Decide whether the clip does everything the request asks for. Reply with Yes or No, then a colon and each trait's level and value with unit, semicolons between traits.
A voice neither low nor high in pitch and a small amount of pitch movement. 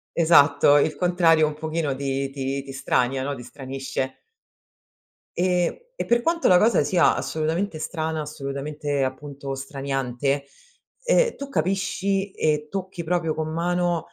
No: medium, 155 Hz; average, 4.4 semitones